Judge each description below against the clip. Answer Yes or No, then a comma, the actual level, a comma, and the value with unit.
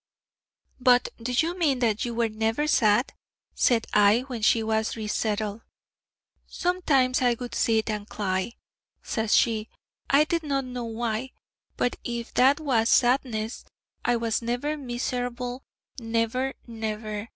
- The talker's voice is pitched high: Yes, high, 235 Hz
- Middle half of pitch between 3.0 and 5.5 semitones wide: No, narrow, 2.5 semitones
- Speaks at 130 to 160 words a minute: Yes, average, 140 wpm